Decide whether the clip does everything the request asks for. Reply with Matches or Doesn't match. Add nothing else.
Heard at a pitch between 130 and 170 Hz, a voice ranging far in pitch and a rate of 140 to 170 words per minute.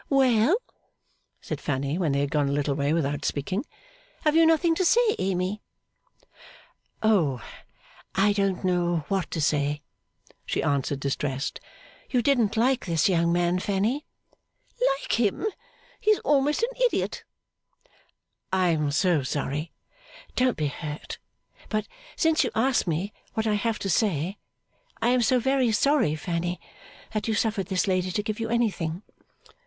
Doesn't match